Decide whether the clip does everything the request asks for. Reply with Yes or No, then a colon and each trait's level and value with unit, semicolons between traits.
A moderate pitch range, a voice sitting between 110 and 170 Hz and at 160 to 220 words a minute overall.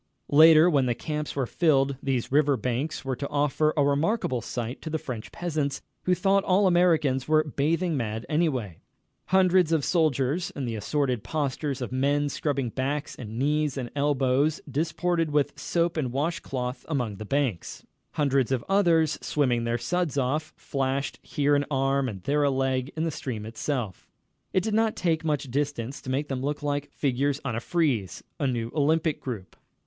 Yes: average, 3.4 semitones; medium, 140 Hz; average, 180 wpm